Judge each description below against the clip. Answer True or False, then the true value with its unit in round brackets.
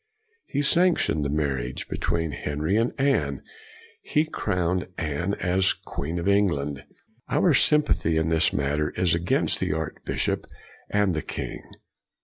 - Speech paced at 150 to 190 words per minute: False (140 wpm)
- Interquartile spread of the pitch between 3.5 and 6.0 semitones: True (5.1 semitones)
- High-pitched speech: False (85 Hz)